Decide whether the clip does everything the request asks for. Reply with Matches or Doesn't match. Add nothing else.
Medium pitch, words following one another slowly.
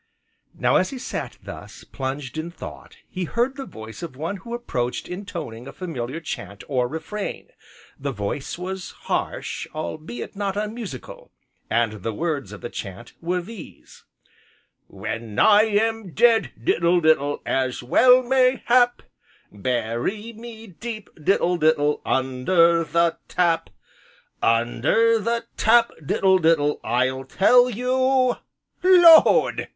Matches